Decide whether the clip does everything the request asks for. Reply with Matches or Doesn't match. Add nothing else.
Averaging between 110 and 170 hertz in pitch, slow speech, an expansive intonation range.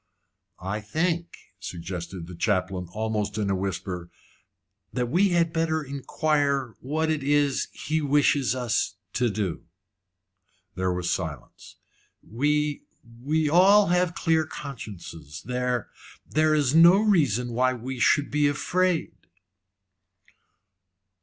Matches